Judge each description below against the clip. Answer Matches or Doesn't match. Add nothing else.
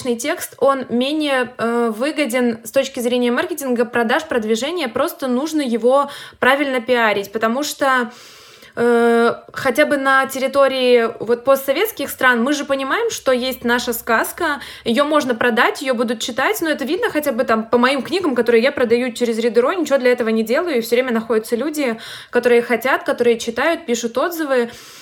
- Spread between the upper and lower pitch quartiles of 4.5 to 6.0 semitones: Doesn't match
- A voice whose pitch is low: Doesn't match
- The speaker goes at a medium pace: Doesn't match